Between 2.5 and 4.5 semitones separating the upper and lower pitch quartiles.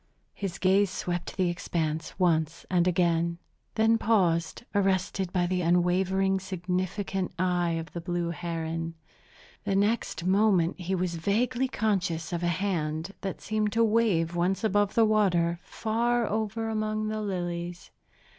Yes: average, 3.2 semitones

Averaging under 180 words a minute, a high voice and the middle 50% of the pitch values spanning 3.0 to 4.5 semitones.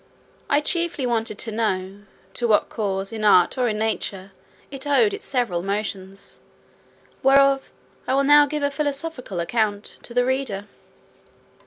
No: average, 150 wpm; high, 235 Hz; wide, 5.5 semitones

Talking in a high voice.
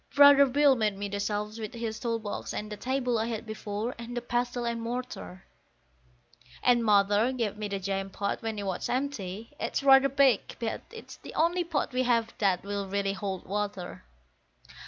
Yes: high, 225 Hz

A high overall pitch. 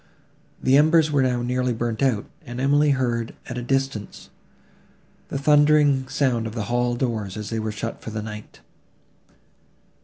No: low, 125 Hz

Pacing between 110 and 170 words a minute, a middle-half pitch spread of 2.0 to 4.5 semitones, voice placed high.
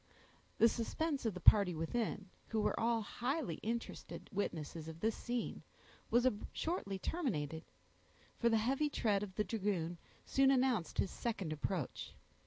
No: average, 145 wpm; average, 5.0 semitones; high, 215 Hz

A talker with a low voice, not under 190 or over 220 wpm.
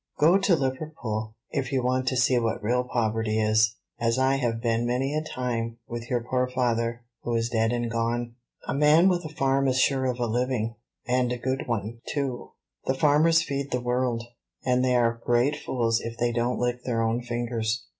Yes: low, 125 Hz; average, 200 wpm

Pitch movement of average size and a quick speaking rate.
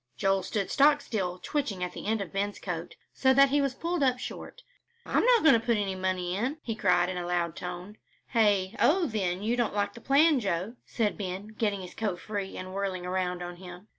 Yes: average, 4.8 semitones; fast, 220 wpm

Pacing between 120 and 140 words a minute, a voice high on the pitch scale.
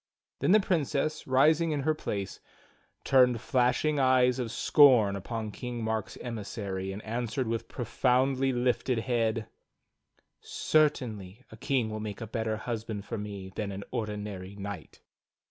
No: slow, 135 wpm; low, 115 Hz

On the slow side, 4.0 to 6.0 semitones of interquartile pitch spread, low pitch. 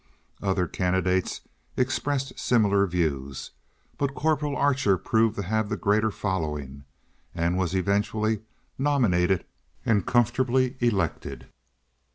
Yes: slow, 105 wpm; average, 5.3 semitones; low, 100 Hz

